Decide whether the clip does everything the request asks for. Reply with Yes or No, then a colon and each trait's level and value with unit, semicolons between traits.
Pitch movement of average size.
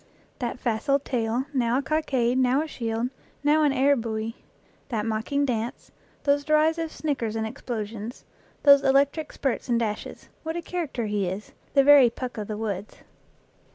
Yes: average, 4.1 semitones